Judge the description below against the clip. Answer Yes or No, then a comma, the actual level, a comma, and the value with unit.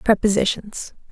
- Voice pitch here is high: Yes, high, 205 Hz